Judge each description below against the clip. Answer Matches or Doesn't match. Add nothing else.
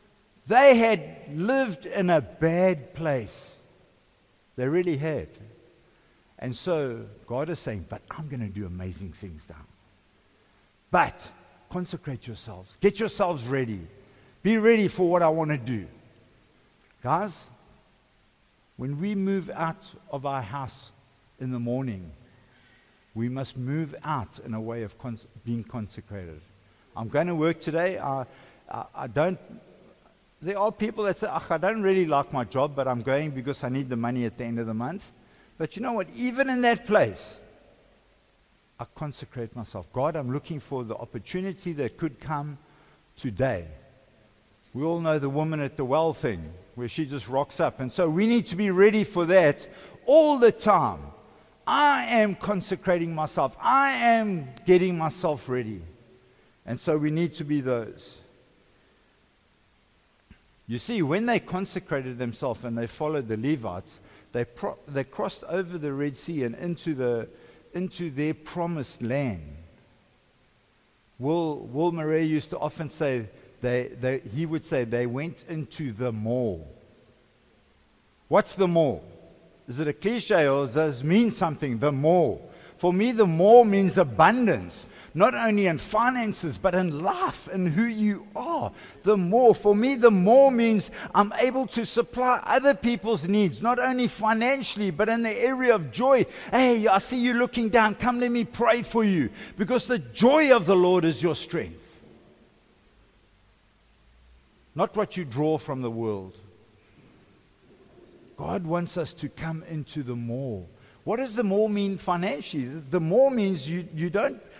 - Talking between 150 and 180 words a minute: Matches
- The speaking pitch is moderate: Matches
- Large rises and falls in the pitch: Matches